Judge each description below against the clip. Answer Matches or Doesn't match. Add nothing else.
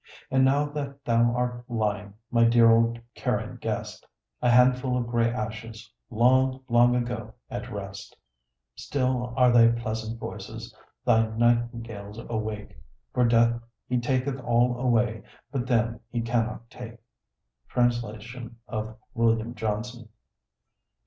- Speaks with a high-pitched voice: Doesn't match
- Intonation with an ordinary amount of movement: Doesn't match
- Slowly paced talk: Matches